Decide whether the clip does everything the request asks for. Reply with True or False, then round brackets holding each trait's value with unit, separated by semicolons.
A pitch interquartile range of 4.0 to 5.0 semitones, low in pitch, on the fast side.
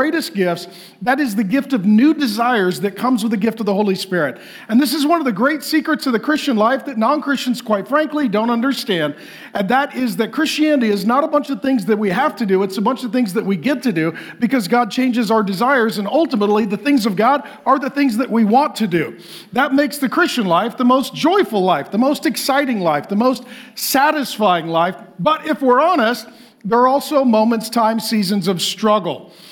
False (4.7 semitones; 240 Hz; 225 wpm)